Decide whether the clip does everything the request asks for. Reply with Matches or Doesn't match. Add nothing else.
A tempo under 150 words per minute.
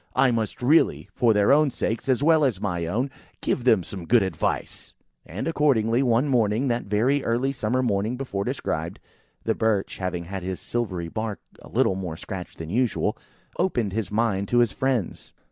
Doesn't match